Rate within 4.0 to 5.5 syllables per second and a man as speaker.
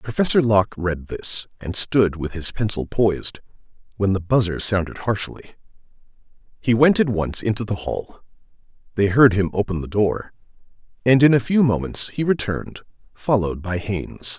Yes: 5.0 syllables/s; male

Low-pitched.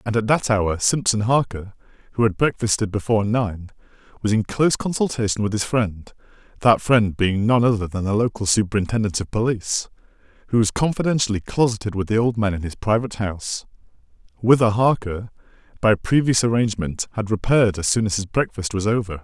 Yes: low, 110 Hz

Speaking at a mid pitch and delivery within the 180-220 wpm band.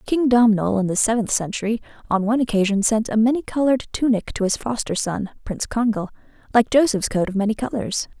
No: high, 225 Hz; average, 190 wpm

